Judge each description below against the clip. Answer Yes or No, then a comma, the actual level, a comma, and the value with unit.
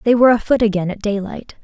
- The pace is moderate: No, fast, 220 wpm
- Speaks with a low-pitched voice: No, high, 215 Hz